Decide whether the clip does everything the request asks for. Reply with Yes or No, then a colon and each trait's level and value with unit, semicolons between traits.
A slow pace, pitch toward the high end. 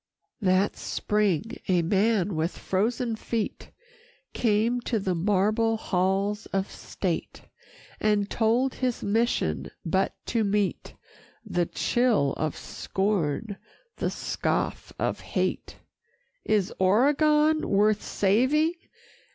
Yes: slow, 105 wpm; high, 210 Hz